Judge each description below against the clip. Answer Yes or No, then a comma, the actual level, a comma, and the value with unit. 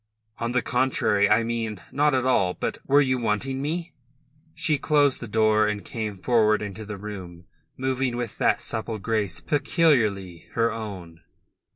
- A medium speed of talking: Yes, average, 160 wpm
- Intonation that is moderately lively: Yes, average, 4.0 semitones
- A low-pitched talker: Yes, low, 115 Hz